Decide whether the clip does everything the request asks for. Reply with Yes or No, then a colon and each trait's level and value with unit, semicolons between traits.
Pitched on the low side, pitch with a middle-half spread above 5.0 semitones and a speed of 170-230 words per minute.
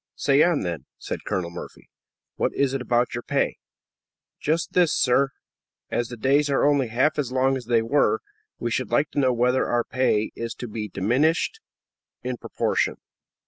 No: low, 130 Hz; average, 3.3 semitones; average, 180 wpm